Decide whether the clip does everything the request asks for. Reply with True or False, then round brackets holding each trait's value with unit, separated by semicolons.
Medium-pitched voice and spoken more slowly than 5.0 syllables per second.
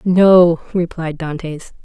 True (170 Hz; 3.2 syllables/s)